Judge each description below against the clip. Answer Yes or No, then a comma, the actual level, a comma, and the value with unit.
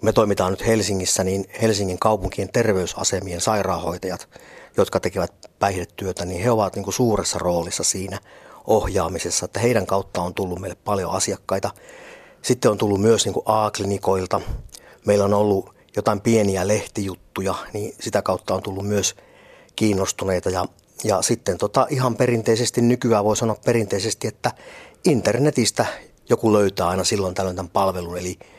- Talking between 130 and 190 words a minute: Yes, average, 145 wpm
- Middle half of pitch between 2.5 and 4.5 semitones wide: Yes, average, 2.8 semitones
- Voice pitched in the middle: No, low, 100 Hz